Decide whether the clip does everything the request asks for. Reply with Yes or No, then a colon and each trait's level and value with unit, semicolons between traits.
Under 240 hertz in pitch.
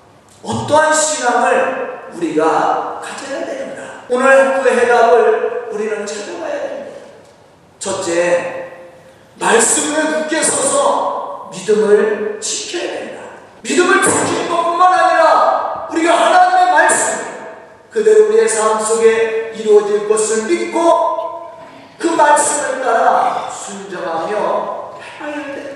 No: very high, 285 Hz